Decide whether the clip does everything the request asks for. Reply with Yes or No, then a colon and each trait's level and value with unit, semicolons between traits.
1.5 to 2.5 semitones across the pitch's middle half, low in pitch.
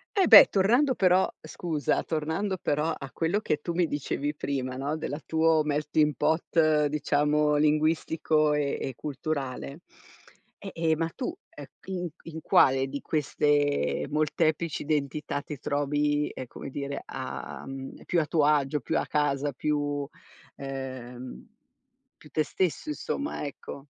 No: narrow, 2.2 semitones; medium, 150 Hz